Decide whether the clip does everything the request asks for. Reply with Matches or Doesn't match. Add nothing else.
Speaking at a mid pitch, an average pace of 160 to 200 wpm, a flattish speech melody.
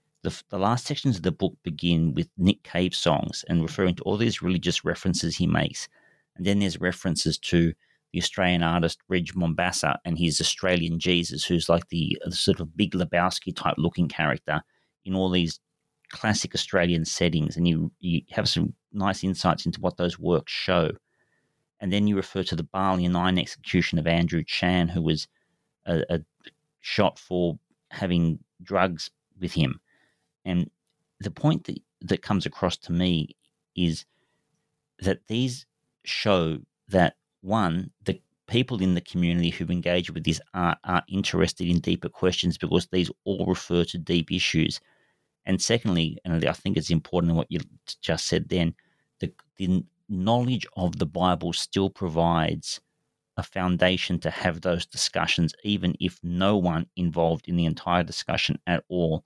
Doesn't match